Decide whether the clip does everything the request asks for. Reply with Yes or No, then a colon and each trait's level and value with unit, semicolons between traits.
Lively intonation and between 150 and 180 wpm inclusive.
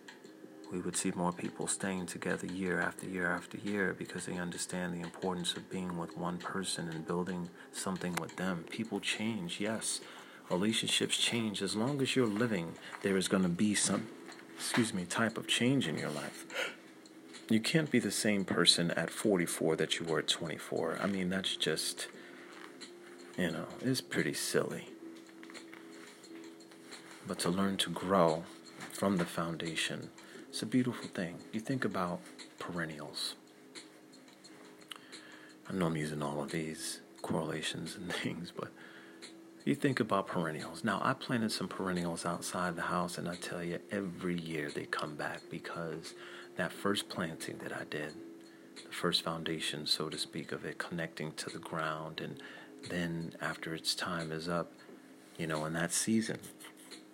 No: average, 3.0 semitones; average, 160 wpm